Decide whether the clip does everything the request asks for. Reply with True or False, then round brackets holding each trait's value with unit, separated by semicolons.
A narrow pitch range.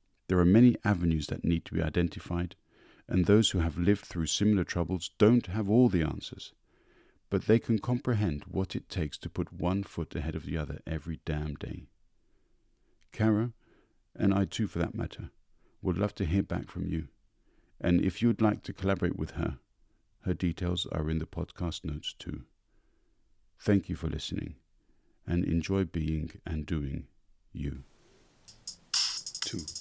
False (3.7 semitones)